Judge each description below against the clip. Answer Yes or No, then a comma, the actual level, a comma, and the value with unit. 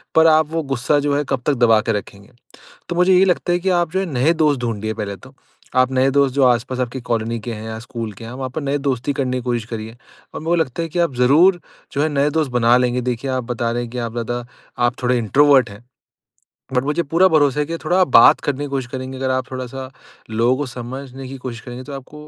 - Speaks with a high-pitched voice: No, low, 130 Hz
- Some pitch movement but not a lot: Yes, average, 3.3 semitones